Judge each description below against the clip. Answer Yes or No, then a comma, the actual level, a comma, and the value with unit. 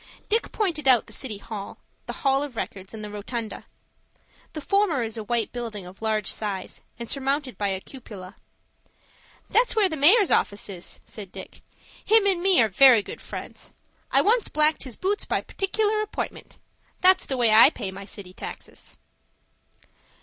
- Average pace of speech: Yes, average, 170 wpm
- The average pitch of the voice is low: No, very high, 250 Hz